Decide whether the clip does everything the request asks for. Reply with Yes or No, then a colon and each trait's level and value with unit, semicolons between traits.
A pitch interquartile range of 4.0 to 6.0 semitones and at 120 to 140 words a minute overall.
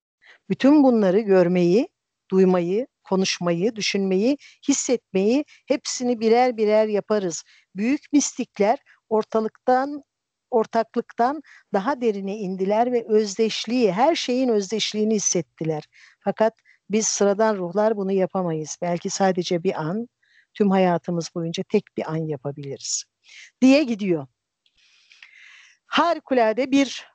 No: average, 4.5 semitones; average, 100 wpm